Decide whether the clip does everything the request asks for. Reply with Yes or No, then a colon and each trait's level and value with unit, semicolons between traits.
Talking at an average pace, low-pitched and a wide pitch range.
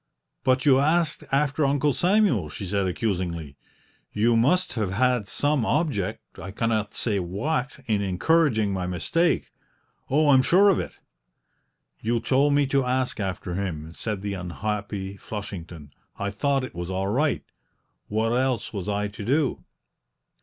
Yes: average, 150 wpm; low, 110 Hz; wide, 6.2 semitones